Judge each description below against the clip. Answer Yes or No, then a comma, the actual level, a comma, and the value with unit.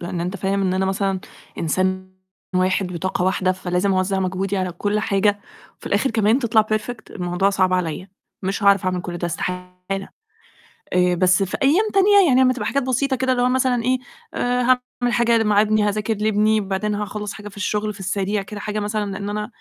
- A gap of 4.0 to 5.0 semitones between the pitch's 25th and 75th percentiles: No, average, 2.7 semitones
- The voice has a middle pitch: No, high, 200 Hz